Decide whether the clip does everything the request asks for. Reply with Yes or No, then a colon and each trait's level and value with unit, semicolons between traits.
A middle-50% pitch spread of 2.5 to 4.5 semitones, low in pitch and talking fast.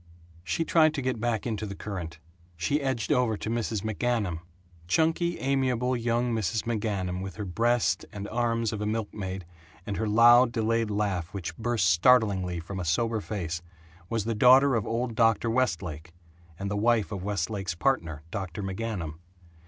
No: average, 3.9 semitones; low, 110 Hz; average, 165 wpm